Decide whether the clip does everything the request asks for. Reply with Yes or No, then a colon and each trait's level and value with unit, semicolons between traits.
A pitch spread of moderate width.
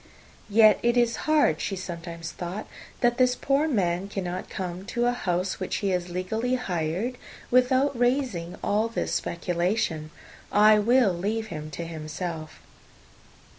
No: wide, 5.7 semitones